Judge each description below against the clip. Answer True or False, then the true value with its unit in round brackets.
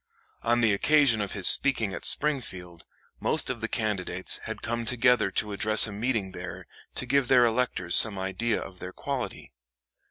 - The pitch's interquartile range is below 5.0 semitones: True (4.4 semitones)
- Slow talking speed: False (170 wpm)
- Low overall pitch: True (110 Hz)